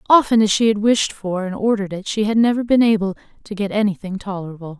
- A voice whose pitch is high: Yes, high, 205 Hz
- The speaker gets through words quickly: Yes, fast, 225 wpm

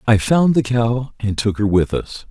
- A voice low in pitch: Yes, low, 115 Hz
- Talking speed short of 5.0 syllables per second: Yes, 4.3 syllables/s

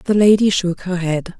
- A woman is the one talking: Yes, female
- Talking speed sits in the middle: No, fast, 215 wpm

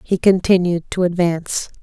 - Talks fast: No, slow, 130 wpm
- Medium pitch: Yes, medium, 180 Hz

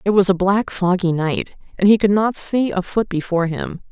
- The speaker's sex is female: Yes, female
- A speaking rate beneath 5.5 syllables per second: Yes, 5.2 syllables/s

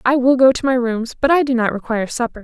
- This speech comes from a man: No, female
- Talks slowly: No, fast, 295 wpm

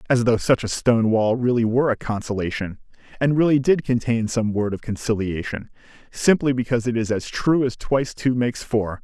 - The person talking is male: Yes, male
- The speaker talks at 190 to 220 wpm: Yes, average, 195 wpm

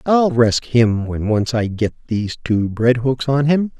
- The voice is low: Yes, low, 120 Hz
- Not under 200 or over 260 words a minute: Yes, fast, 205 wpm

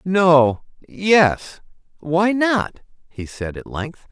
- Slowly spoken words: Yes, slow, 85 wpm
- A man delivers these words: Yes, male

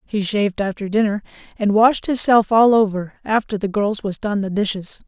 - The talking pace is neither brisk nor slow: Yes, average, 190 wpm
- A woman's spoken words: Yes, female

